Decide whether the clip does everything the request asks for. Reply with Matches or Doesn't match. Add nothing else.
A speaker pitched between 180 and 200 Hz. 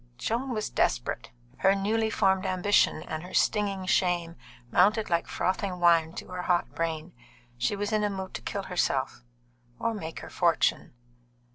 Matches